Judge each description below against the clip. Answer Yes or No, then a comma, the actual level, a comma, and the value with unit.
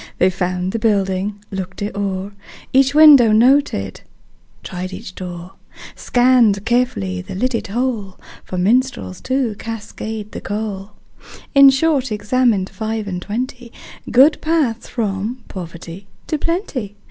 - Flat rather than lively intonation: No, average, 5.0 semitones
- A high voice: Yes, high, 215 Hz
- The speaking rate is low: Yes, slow, 125 wpm